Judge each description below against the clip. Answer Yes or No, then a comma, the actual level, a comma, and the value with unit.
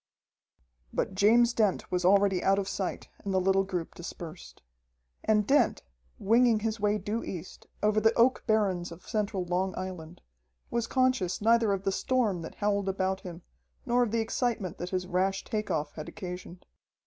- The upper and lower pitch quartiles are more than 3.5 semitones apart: No, average, 3.2 semitones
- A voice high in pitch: Yes, high, 195 Hz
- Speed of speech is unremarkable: Yes, average, 170 wpm